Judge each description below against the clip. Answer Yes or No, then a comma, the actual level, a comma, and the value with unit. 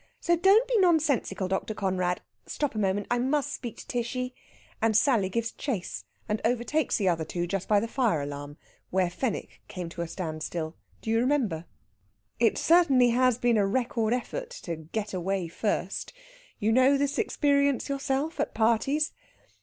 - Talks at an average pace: Yes, average, 170 wpm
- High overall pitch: Yes, high, 225 Hz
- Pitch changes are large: Yes, wide, 6.4 semitones